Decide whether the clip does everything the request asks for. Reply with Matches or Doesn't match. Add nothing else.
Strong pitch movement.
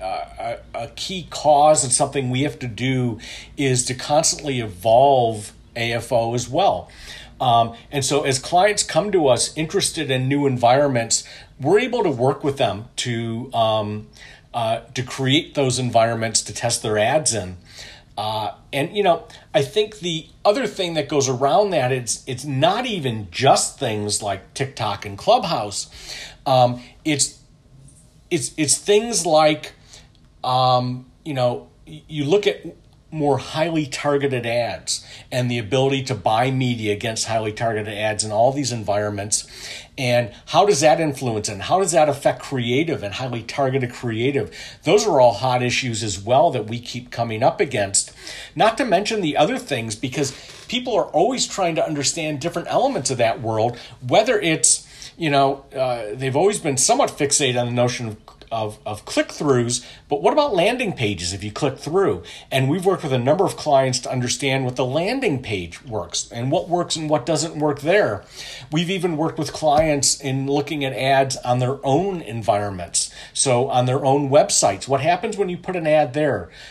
Doesn't match